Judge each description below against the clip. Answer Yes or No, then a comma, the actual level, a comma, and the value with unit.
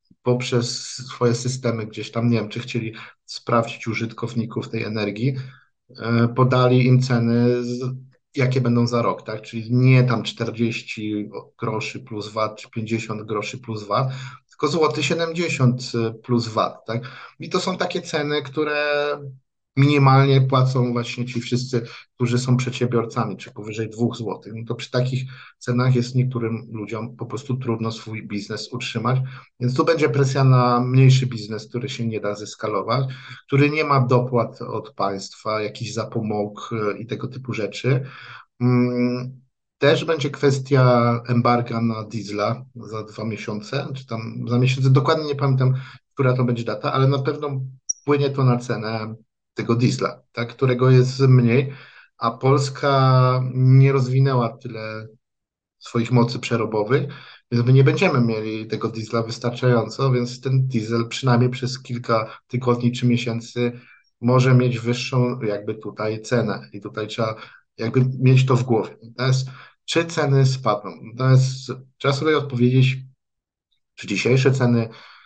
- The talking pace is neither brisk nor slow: Yes, average, 140 wpm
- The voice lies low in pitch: Yes, low, 120 Hz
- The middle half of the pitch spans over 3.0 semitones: No, narrow, 2.4 semitones